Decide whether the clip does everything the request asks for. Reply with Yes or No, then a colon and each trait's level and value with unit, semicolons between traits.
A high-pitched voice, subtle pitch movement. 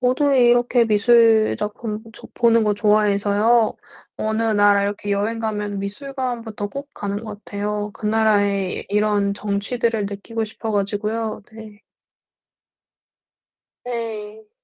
Yes: high, 215 Hz; narrow, 1.9 semitones